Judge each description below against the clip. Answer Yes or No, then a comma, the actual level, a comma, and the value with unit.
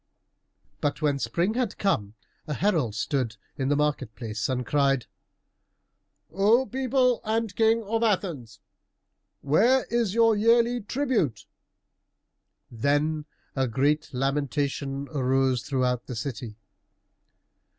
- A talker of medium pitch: Yes, medium, 150 Hz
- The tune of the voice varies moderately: No, wide, 9.0 semitones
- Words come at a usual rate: No, slow, 110 wpm